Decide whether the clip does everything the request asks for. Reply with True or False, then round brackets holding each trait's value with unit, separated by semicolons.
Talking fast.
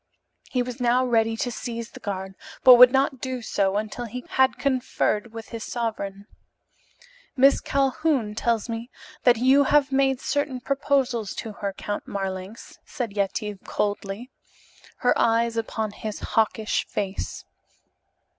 False (140 wpm)